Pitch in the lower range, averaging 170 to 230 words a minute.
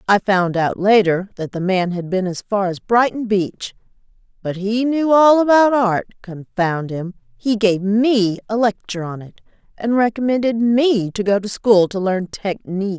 No: high, 205 Hz; average, 180 wpm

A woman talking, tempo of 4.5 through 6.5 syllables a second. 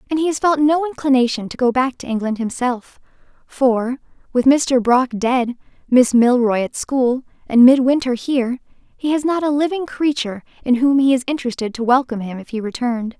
Yes: female; 5.4 syllables/s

